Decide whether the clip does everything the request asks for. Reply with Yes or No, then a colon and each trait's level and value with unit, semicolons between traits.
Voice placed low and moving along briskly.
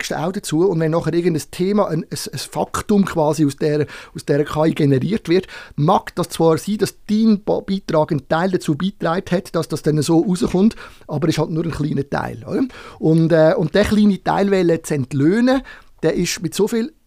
No: medium, 165 Hz; fast, 200 wpm